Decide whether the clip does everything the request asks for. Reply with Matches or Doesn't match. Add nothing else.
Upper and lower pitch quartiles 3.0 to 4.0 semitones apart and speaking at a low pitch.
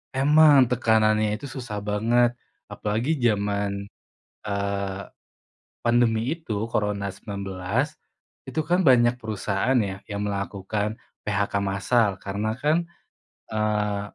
Matches